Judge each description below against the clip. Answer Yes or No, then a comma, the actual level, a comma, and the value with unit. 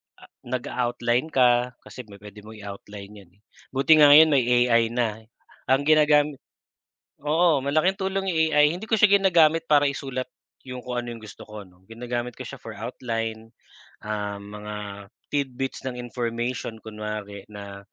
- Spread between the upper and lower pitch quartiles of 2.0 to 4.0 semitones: No, average, 5.2 semitones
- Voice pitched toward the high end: No, low, 120 Hz